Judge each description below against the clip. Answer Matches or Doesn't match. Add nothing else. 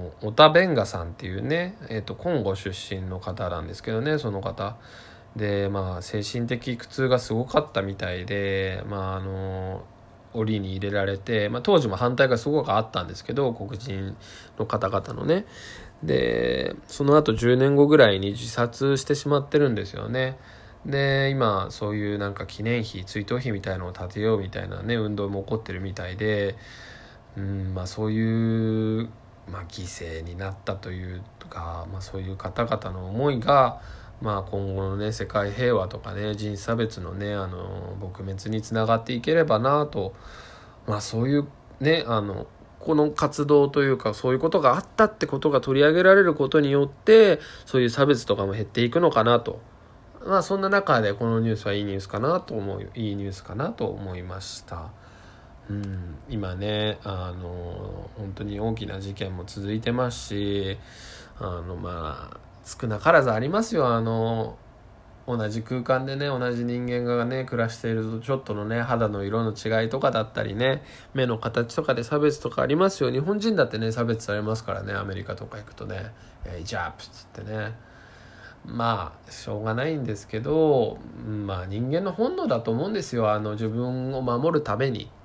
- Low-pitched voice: Matches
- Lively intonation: Doesn't match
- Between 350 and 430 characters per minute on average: Doesn't match